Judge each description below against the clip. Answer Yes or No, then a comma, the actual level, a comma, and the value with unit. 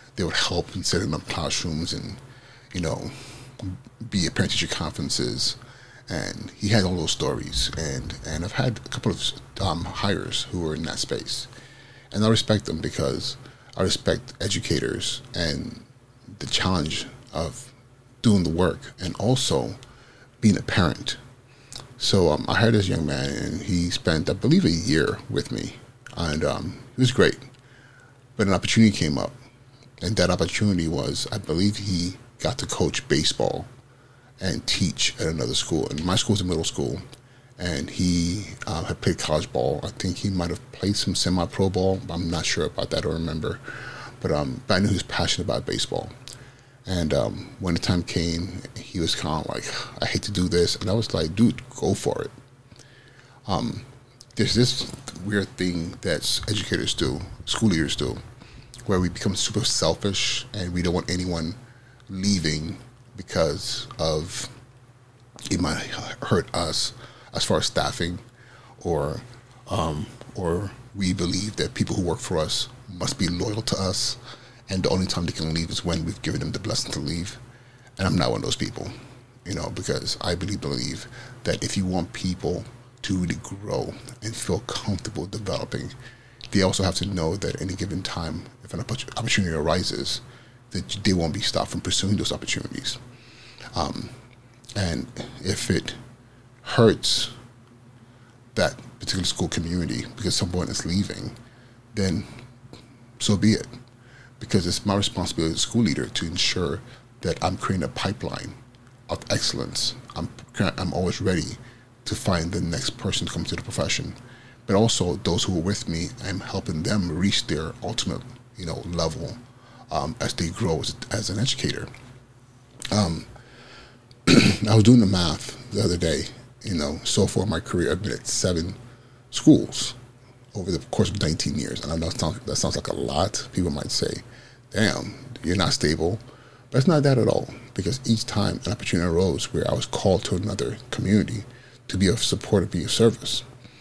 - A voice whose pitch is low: Yes, low, 115 Hz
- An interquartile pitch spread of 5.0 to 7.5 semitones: Yes, average, 5.3 semitones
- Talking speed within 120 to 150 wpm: No, average, 175 wpm